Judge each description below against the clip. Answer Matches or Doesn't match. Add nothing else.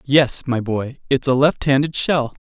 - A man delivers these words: Matches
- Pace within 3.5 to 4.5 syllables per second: Matches